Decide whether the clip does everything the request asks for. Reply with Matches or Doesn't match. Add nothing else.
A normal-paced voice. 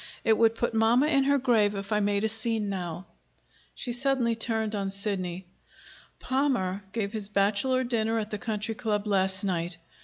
Matches